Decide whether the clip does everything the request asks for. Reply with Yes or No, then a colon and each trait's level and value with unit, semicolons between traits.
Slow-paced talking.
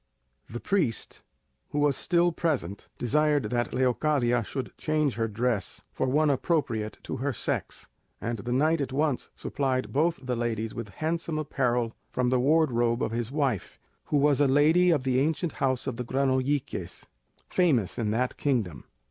No: average, 165 wpm